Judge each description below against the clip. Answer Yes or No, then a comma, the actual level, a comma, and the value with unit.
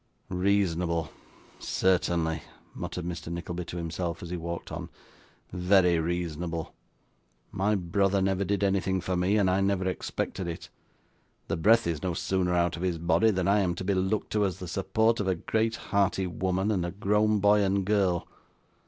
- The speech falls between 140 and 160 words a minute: No, average, 175 wpm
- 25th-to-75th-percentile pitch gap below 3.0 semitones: Yes, narrow, 2.4 semitones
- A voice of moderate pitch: No, very low, 95 Hz